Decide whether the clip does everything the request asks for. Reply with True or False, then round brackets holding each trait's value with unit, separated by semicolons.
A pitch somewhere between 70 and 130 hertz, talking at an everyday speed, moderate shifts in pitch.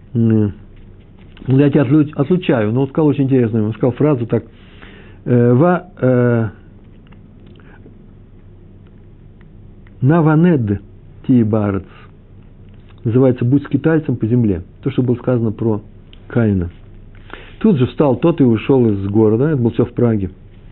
True (110 Hz; 120 wpm; 4.3 semitones)